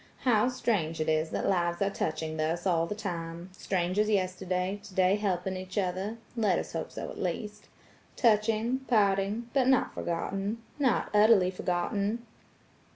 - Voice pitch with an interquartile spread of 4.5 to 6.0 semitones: No, average, 3.5 semitones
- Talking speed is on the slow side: Yes, slow, 120 wpm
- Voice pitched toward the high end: Yes, high, 195 Hz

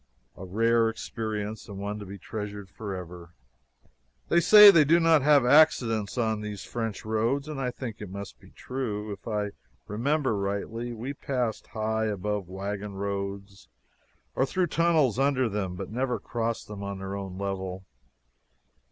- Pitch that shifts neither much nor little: Yes, average, 4.0 semitones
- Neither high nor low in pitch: No, low, 110 Hz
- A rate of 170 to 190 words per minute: No, average, 160 wpm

